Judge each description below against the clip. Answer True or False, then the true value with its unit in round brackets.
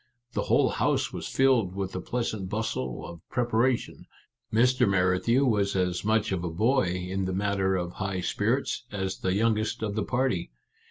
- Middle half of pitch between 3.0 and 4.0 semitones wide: True (3.7 semitones)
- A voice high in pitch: False (100 Hz)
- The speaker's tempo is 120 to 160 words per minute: False (170 wpm)